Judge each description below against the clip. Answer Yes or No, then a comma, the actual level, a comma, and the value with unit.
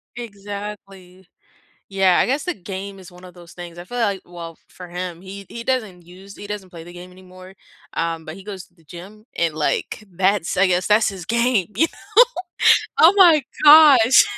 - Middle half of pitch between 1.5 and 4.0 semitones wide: Yes, average, 2.9 semitones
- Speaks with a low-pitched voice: No, high, 190 Hz